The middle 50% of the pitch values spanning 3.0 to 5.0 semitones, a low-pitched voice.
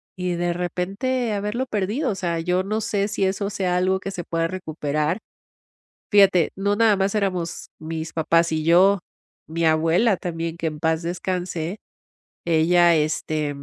No: average, 3.3 semitones; medium, 180 Hz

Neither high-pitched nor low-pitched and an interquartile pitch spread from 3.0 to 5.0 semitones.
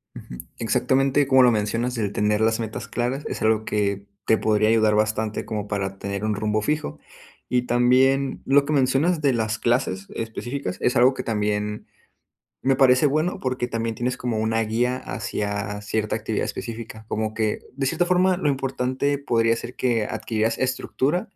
No: low, 115 Hz; average, 3.5 semitones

